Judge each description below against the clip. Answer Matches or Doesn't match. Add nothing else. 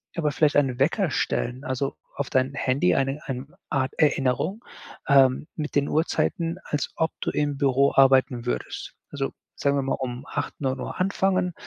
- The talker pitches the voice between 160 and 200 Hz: Doesn't match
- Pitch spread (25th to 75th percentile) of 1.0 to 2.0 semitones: Doesn't match